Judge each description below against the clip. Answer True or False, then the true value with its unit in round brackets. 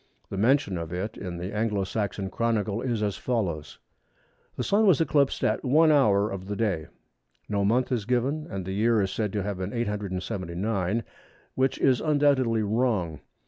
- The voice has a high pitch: False (105 Hz)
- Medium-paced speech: True (170 wpm)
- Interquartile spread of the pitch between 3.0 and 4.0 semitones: False (4.5 semitones)